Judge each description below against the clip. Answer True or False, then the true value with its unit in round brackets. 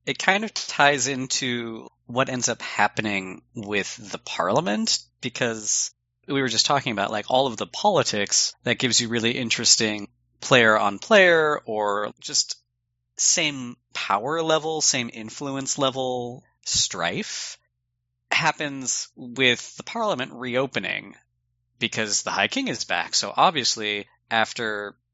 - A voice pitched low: True (120 Hz)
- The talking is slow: True (130 wpm)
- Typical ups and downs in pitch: True (3.8 semitones)